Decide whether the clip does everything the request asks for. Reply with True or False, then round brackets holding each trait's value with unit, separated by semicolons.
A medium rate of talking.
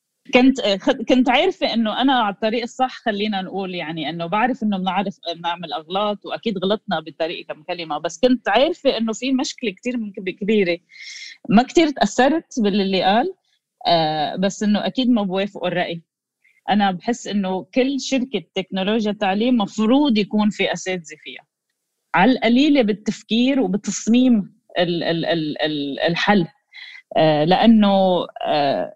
True (120 wpm)